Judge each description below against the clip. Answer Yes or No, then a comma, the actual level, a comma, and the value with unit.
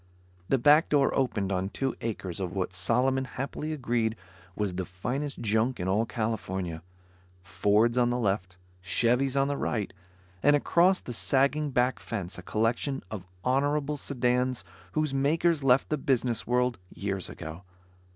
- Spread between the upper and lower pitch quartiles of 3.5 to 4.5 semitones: No, wide, 5.6 semitones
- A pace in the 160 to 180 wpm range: No, average, 150 wpm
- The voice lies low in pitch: Yes, low, 120 Hz